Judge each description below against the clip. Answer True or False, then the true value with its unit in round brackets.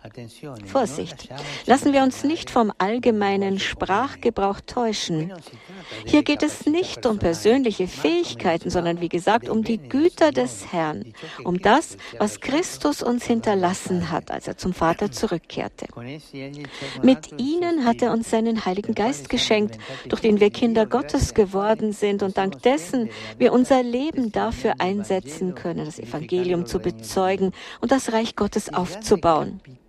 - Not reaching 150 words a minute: True (140 wpm)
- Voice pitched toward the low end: False (205 Hz)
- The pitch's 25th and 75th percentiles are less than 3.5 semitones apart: False (5.3 semitones)